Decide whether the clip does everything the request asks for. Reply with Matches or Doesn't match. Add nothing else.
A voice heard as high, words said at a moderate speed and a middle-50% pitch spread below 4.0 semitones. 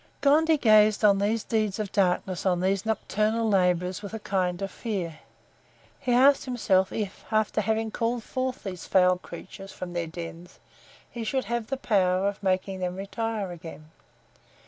Matches